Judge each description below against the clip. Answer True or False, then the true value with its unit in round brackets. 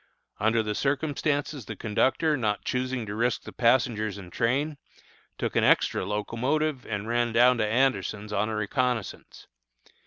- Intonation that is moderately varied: True (3.7 semitones)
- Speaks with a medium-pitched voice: False (120 Hz)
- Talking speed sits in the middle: True (150 wpm)